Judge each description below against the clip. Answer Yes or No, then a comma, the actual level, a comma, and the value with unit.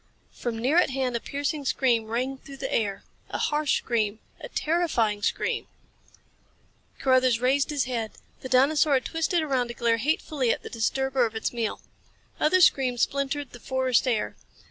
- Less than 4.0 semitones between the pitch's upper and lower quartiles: Yes, average, 3.3 semitones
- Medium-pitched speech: No, very high, 260 Hz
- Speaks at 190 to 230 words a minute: No, average, 165 wpm